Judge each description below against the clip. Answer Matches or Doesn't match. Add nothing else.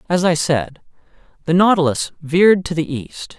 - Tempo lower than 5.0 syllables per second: Matches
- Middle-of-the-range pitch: Matches